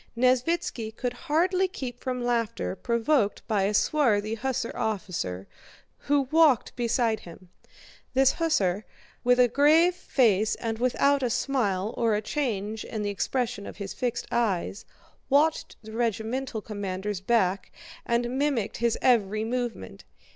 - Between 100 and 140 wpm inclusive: Yes, slow, 135 wpm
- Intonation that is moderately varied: Yes, average, 4.0 semitones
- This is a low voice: No, high, 235 Hz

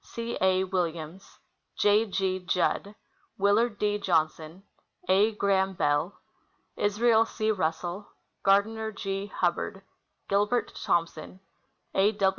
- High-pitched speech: Yes, high, 195 Hz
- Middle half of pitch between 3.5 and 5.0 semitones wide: No, narrow, 2.4 semitones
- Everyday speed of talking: No, slow, 100 wpm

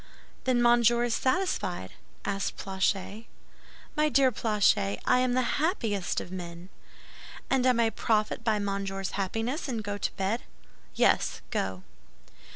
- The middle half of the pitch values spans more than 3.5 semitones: Yes, average, 4.2 semitones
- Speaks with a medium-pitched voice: No, high, 220 Hz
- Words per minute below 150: Yes, slow, 135 wpm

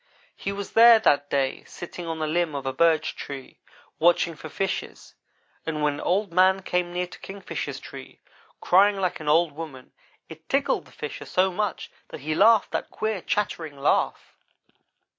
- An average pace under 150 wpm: No, average, 170 wpm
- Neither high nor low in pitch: Yes, medium, 175 Hz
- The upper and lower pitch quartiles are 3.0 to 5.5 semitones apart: Yes, average, 4.0 semitones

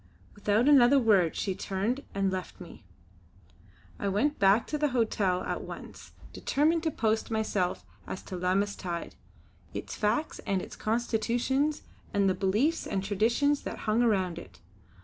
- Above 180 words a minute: No, average, 150 wpm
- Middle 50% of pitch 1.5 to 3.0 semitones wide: No, average, 4.7 semitones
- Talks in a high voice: Yes, high, 215 Hz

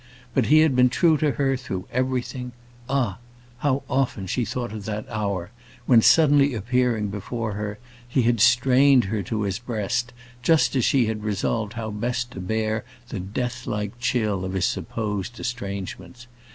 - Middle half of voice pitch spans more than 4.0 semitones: No, average, 3.4 semitones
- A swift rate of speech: No, average, 165 wpm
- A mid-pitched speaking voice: No, low, 115 Hz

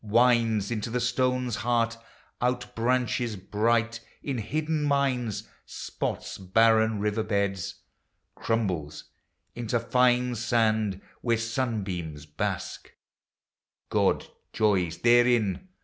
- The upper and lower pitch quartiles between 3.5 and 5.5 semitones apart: No, average, 2.8 semitones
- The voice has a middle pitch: No, low, 115 Hz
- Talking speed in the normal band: No, slow, 95 wpm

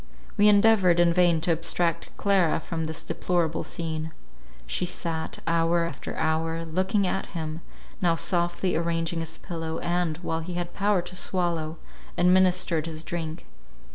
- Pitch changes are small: Yes, narrow, 1.8 semitones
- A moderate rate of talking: Yes, average, 145 wpm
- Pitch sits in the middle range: Yes, medium, 170 Hz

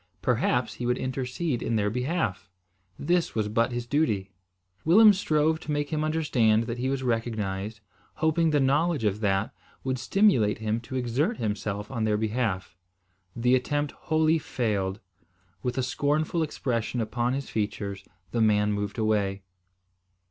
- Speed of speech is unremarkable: Yes, average, 150 wpm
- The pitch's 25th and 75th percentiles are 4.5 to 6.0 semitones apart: Yes, wide, 5.4 semitones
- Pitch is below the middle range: Yes, low, 120 Hz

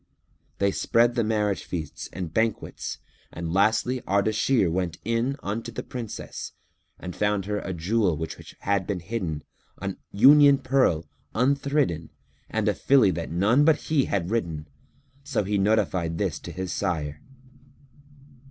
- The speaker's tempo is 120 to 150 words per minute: Yes, average, 145 wpm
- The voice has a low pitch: Yes, low, 100 Hz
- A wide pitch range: No, average, 5.0 semitones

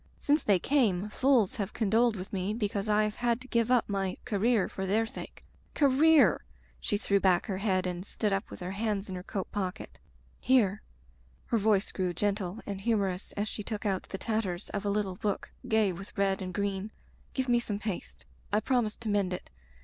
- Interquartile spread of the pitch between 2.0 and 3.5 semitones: Yes, narrow, 2.6 semitones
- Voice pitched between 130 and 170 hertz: No, high, 205 Hz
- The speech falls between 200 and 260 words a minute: Yes, fast, 205 wpm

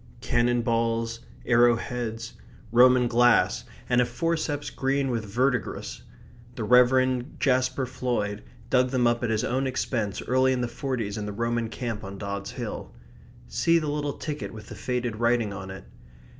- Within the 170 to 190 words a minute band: No, average, 160 wpm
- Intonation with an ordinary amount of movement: No, narrow, 2.2 semitones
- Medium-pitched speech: No, low, 120 Hz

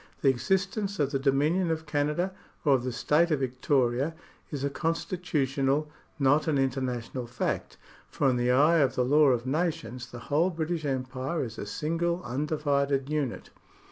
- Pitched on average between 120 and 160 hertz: Yes, medium, 140 Hz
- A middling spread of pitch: Yes, average, 3.6 semitones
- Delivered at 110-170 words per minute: Yes, average, 165 wpm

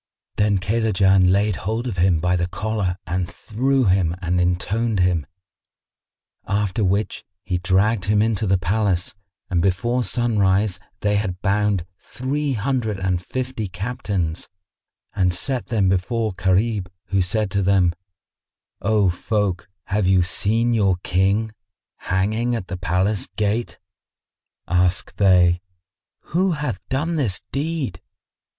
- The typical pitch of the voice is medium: No, low, 100 Hz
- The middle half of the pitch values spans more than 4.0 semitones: No, average, 3.4 semitones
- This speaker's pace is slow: Yes, slow, 130 wpm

